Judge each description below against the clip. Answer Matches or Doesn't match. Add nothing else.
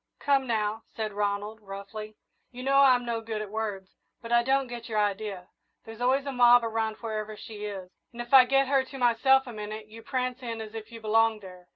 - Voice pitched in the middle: Doesn't match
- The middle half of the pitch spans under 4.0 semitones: Matches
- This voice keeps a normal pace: Doesn't match